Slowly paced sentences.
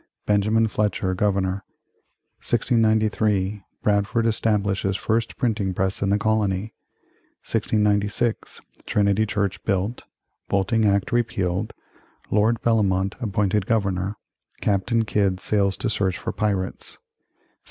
Yes: slow, 105 wpm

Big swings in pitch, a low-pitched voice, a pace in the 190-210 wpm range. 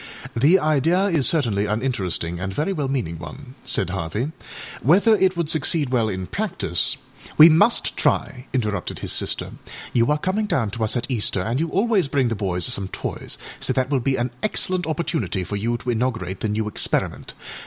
Yes: wide, 7.4 semitones; low, 130 Hz; average, 195 wpm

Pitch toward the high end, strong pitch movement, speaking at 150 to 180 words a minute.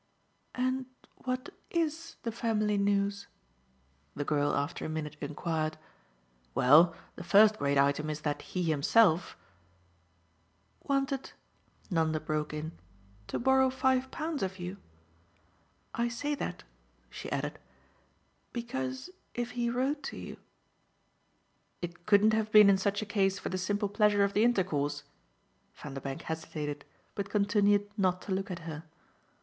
No: high, 195 Hz; wide, 6.9 semitones; average, 140 wpm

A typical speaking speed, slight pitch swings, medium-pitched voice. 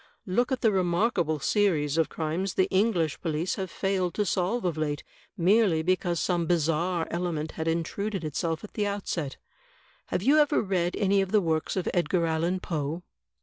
No: average, 175 wpm; average, 3.3 semitones; medium, 175 Hz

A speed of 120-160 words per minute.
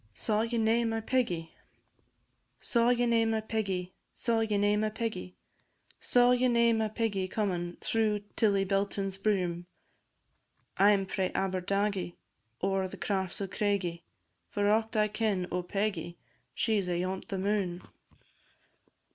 Yes: average, 140 wpm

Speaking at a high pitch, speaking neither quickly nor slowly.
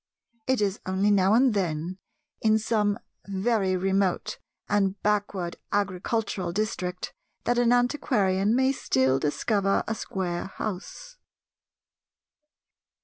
No: high, 200 Hz; slow, 105 wpm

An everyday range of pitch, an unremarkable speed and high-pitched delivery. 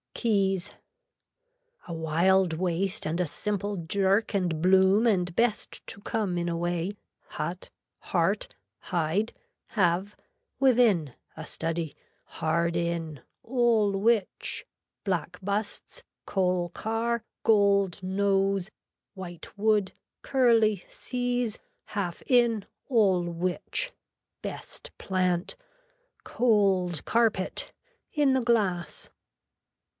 No: average, 4.0 semitones; slow, 100 wpm; high, 195 Hz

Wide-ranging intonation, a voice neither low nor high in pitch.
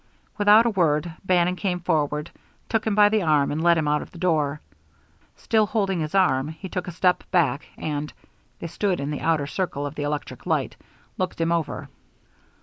No: average, 3.9 semitones; medium, 170 Hz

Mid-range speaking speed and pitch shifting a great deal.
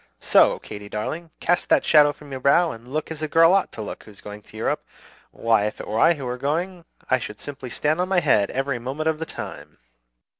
No: fast, 235 wpm; wide, 6.1 semitones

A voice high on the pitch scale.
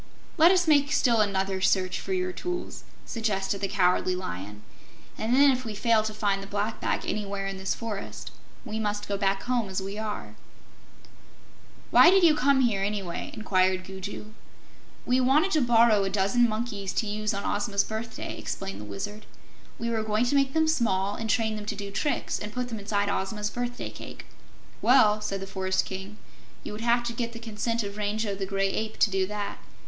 Yes: high, 210 Hz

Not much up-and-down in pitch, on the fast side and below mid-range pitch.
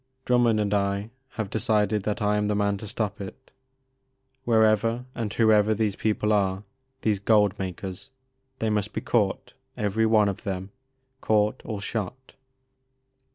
No: narrow, 1.9 semitones; average, 160 wpm; low, 105 Hz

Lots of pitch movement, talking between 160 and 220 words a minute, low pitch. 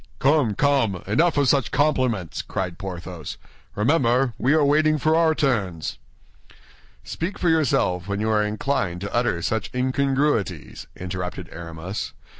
No: wide, 7.5 semitones; slow, 135 wpm; low, 115 Hz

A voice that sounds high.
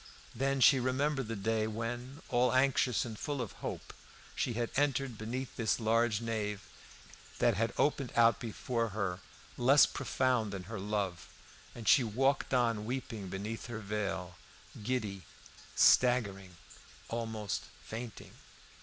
No: low, 115 Hz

